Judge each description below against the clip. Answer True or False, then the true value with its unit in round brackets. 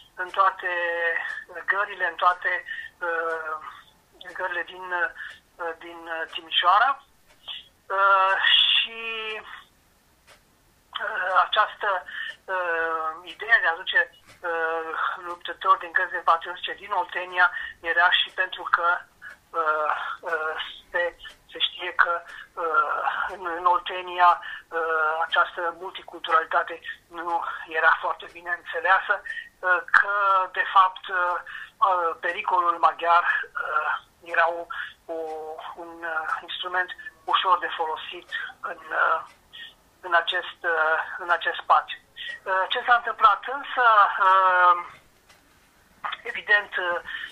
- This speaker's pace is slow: True (105 wpm)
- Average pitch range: True (3.9 semitones)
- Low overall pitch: False (180 Hz)